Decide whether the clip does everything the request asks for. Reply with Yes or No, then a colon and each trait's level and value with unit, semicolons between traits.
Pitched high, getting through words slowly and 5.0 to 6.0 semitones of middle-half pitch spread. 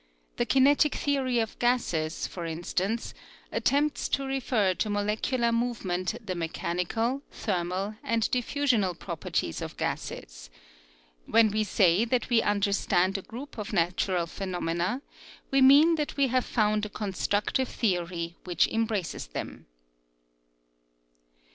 Yes: high, 210 Hz; slow, 130 wpm; wide, 5.4 semitones